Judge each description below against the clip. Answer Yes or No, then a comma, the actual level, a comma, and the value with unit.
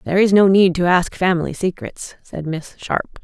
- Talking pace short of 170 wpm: No, fast, 205 wpm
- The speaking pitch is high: No, medium, 180 Hz